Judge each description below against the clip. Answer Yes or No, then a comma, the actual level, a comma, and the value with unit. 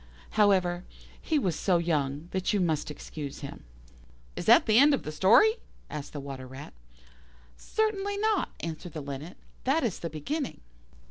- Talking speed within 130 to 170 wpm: Yes, average, 160 wpm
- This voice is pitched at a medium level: Yes, medium, 175 Hz